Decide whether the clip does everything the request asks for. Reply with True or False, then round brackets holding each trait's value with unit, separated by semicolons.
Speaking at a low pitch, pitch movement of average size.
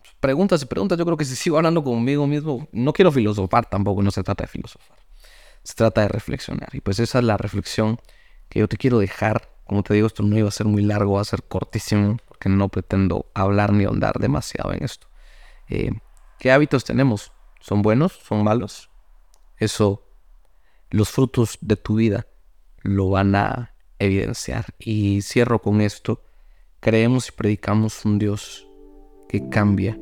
True (105 Hz; 3.2 semitones)